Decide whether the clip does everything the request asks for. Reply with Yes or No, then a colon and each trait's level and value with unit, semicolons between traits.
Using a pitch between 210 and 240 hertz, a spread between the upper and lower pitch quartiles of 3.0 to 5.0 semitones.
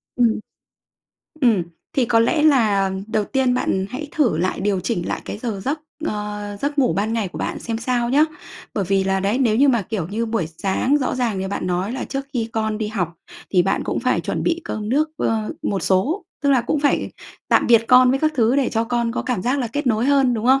Yes: high, 230 Hz; average, 4.4 semitones